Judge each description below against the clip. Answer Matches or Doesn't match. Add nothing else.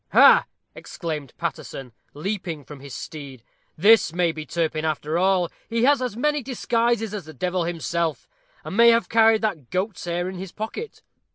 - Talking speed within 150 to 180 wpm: Matches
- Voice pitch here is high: Doesn't match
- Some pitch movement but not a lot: Doesn't match